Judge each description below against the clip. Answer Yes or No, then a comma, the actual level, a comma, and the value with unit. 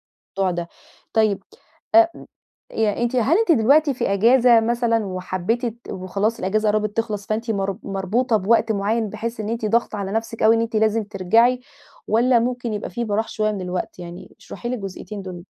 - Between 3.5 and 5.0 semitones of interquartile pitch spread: No, average, 2.9 semitones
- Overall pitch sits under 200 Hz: No, high, 220 Hz